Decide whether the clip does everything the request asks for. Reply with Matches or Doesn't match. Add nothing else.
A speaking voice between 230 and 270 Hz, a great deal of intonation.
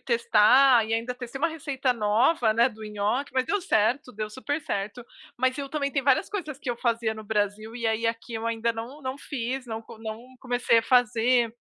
Doesn't match